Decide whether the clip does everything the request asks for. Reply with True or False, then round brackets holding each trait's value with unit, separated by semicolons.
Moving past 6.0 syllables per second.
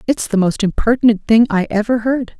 False (5.5 syllables/s)